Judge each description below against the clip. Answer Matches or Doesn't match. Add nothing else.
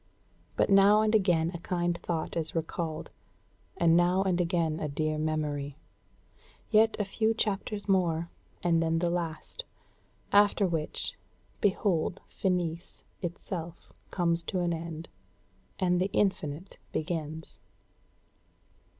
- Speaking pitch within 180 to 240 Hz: Doesn't match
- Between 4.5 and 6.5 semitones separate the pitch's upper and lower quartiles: Doesn't match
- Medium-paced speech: Doesn't match